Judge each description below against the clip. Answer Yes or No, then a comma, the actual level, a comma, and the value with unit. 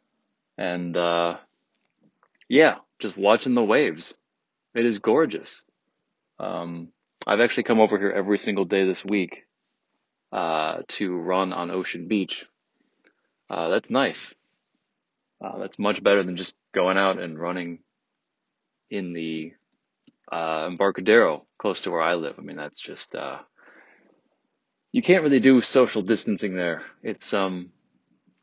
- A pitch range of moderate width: Yes, average, 3.0 semitones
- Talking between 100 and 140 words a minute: Yes, slow, 135 wpm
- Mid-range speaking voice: No, very low, 95 Hz